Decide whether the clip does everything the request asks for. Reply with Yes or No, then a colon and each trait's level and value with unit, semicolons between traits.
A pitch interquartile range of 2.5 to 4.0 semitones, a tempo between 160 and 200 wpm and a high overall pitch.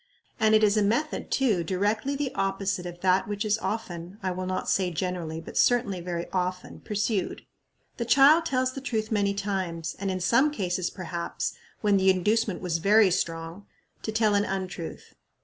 Yes: average, 3.2 semitones; average, 180 wpm; high, 195 Hz